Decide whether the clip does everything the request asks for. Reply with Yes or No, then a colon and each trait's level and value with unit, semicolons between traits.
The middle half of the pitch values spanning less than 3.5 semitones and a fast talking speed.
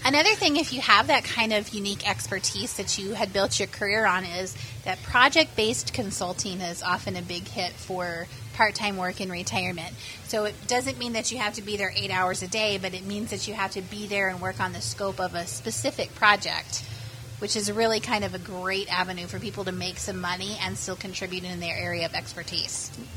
Yes: average, 3.0 semitones; fast, 220 wpm